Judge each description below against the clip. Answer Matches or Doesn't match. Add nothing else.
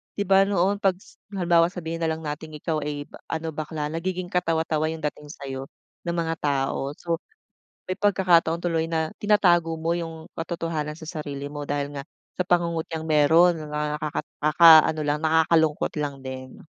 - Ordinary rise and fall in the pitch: Doesn't match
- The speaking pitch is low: Doesn't match